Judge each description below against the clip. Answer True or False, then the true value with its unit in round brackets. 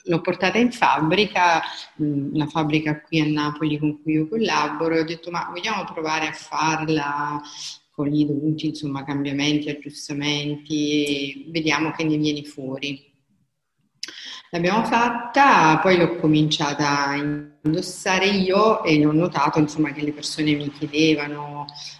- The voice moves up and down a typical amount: False (2.0 semitones)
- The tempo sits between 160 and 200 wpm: False (135 wpm)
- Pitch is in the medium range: True (150 Hz)